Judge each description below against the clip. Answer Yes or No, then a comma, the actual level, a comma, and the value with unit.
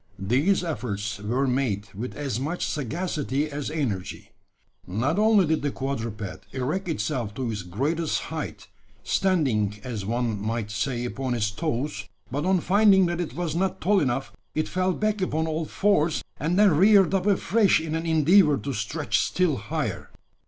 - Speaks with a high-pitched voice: No, medium, 145 Hz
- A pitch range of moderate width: No, wide, 7.2 semitones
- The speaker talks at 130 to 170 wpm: Yes, average, 165 wpm